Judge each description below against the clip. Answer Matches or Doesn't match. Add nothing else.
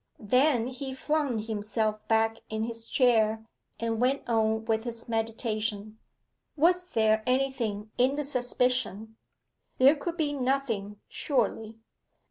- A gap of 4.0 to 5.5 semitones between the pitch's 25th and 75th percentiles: Doesn't match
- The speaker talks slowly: Matches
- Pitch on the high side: Matches